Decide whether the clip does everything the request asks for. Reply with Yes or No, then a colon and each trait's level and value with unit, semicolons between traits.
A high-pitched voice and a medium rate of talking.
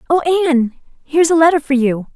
Yes: very high, 295 Hz; average, 195 wpm